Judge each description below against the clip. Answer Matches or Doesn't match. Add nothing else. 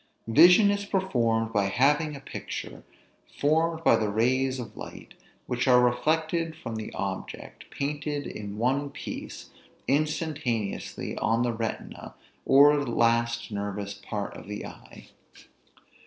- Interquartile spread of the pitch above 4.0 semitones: Matches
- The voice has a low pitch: Matches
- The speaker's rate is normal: Doesn't match